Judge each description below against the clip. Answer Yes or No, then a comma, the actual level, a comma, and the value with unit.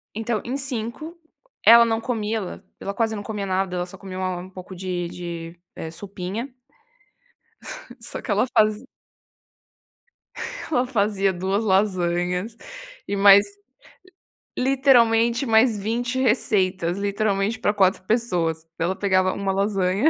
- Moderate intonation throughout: Yes, average, 3.5 semitones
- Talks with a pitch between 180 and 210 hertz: Yes, high, 200 Hz